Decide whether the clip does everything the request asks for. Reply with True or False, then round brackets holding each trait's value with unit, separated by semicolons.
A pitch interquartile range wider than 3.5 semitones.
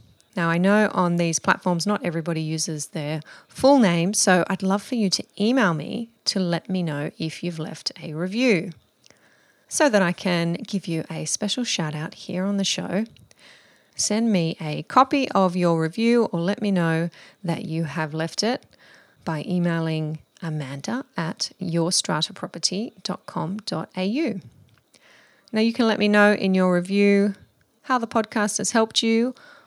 True (4.1 semitones)